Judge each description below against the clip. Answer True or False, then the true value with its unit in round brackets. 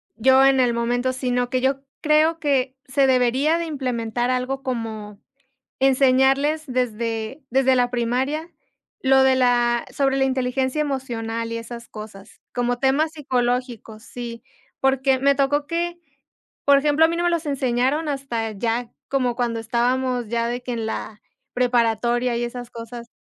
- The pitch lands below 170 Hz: False (255 Hz)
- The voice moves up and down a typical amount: False (2.3 semitones)